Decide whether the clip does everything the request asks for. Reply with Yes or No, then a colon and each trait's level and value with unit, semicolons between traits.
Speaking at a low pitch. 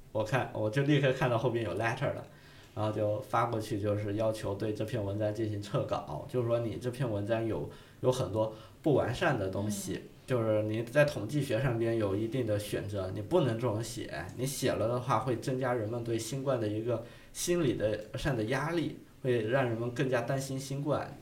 Yes: low, 120 Hz